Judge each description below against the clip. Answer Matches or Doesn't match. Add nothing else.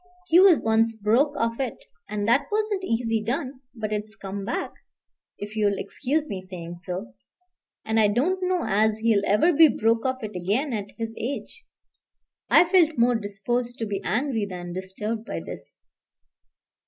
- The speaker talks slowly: Doesn't match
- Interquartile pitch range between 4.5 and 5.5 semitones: Matches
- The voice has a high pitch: Matches